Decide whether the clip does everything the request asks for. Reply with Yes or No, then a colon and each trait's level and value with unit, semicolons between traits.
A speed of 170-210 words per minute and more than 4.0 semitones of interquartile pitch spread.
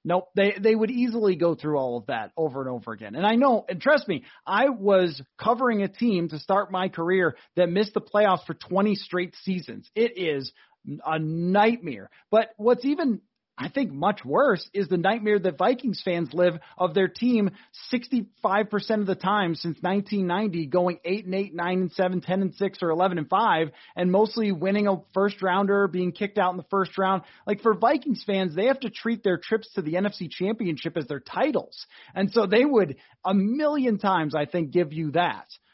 No: average, 200 wpm; average, 3.4 semitones